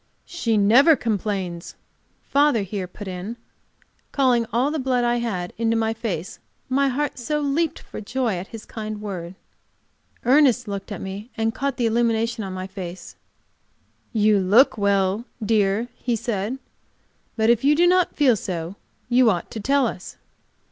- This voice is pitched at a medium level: No, high, 225 Hz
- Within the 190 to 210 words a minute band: No, average, 160 wpm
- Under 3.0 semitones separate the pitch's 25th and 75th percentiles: No, average, 4.2 semitones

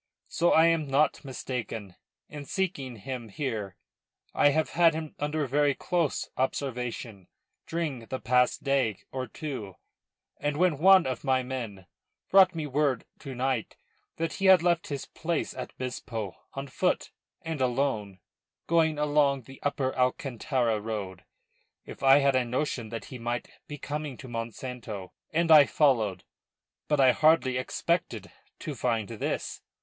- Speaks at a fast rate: No, average, 145 wpm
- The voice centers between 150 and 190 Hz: No, low, 135 Hz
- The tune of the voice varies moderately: Yes, average, 4.2 semitones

